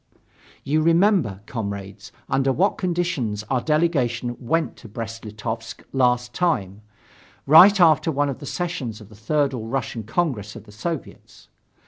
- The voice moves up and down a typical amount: No, wide, 6.5 semitones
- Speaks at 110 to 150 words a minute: Yes, average, 145 wpm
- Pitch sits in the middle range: No, low, 125 Hz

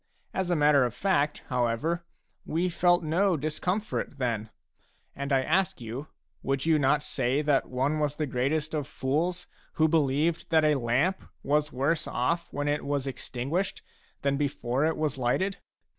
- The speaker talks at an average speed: Yes, average, 160 wpm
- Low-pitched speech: No, medium, 150 Hz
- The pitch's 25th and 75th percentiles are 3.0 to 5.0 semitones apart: Yes, average, 3.4 semitones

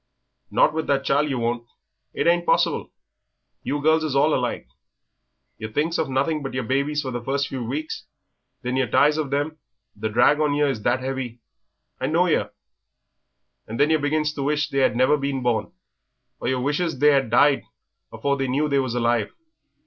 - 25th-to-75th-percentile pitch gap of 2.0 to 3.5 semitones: Yes, average, 2.9 semitones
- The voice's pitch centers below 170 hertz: Yes, medium, 140 Hz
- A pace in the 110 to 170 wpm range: No, average, 195 wpm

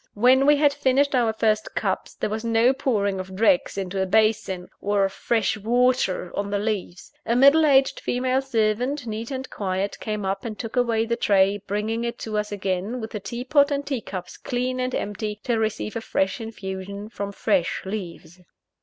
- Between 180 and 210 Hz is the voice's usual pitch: No, high, 220 Hz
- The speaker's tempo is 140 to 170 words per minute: No, average, 195 wpm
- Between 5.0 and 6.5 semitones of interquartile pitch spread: No, average, 3.8 semitones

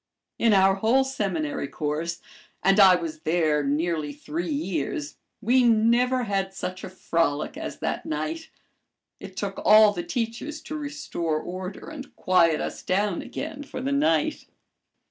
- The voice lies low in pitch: No, high, 195 Hz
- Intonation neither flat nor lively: No, wide, 7.7 semitones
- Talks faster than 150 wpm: No, average, 145 wpm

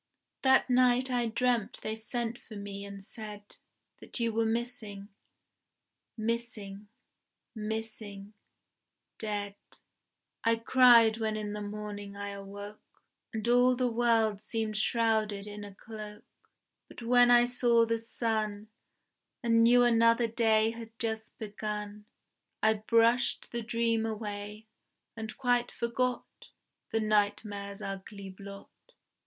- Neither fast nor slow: No, slow, 120 wpm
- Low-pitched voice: No, high, 220 Hz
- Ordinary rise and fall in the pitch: No, narrow, 2.0 semitones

